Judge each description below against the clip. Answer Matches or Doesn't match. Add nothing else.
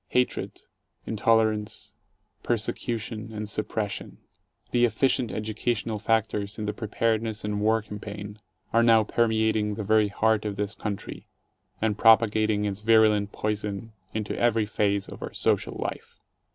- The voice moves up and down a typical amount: Doesn't match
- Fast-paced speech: Doesn't match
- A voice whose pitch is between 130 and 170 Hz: Doesn't match